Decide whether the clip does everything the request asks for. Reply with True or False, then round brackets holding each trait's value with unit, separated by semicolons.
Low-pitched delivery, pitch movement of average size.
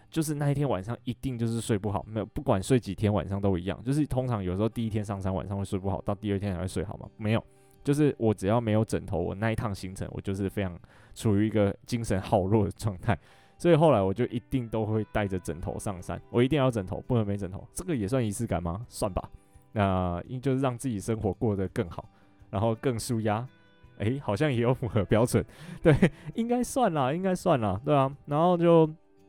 True (110 Hz; 4.8 semitones)